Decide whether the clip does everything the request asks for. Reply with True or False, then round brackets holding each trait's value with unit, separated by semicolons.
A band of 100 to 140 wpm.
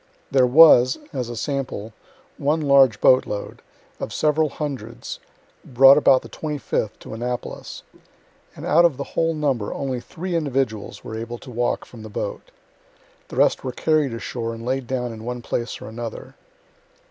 False (165 wpm)